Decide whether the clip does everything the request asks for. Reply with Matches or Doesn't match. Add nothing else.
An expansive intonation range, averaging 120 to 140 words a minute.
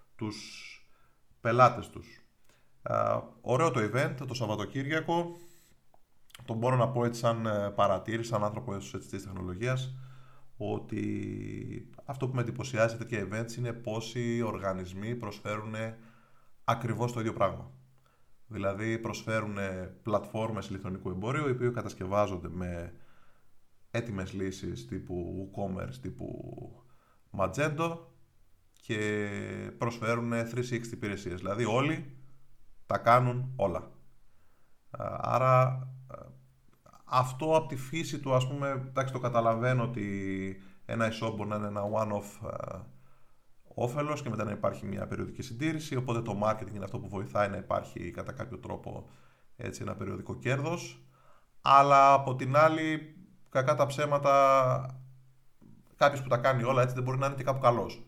Doesn't match